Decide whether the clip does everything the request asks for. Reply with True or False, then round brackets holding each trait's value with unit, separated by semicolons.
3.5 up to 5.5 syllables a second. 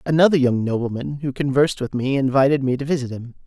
False (6.5 syllables/s)